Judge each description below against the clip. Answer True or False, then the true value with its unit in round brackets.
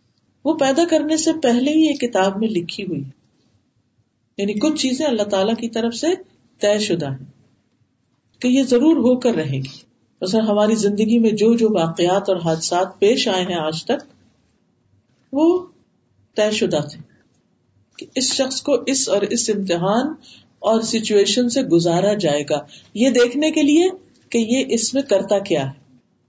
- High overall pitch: True (215 Hz)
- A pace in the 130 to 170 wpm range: True (165 wpm)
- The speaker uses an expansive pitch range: True (7.2 semitones)